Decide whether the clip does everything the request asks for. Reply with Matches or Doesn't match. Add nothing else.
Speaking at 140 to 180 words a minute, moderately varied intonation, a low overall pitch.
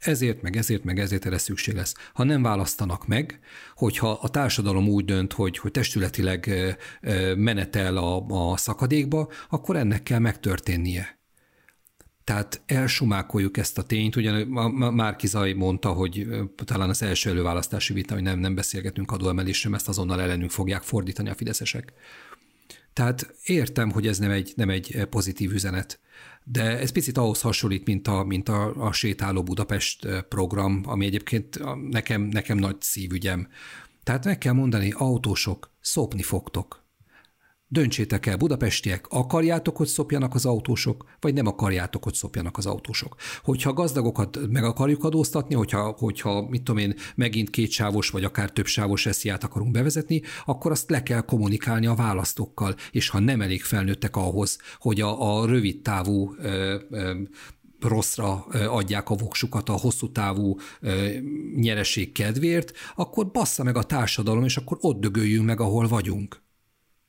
Matches